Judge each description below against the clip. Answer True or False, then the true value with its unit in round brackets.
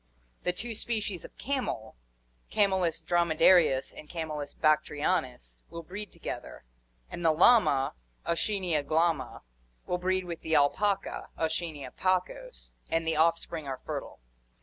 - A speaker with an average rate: False (125 wpm)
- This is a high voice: False (165 Hz)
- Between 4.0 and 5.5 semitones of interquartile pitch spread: False (3.5 semitones)